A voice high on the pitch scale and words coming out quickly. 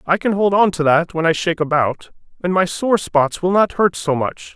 No: medium, 175 Hz; fast, 250 wpm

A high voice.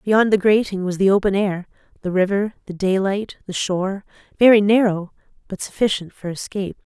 Yes: high, 195 Hz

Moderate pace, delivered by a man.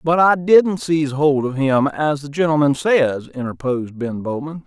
Yes: average, 180 wpm; male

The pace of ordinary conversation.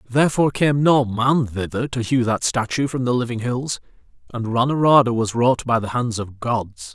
Yes: average, 190 wpm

